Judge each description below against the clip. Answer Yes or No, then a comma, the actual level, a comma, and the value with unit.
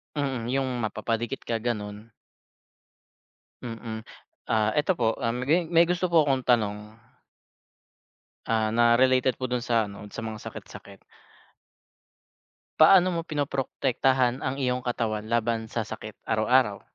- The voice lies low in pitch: Yes, low, 120 Hz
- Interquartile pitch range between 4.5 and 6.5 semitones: No, average, 3.2 semitones